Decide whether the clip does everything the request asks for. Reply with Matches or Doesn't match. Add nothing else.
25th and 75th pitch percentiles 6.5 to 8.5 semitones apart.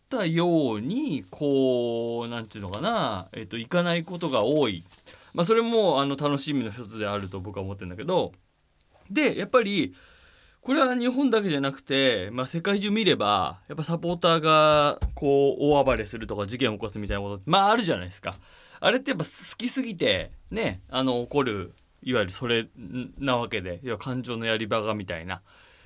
Matches